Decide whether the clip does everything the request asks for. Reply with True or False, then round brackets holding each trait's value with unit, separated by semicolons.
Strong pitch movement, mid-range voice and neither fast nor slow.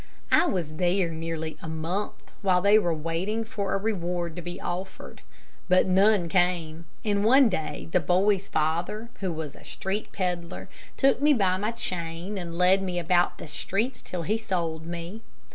False (3.3 semitones; 180 Hz; 175 wpm)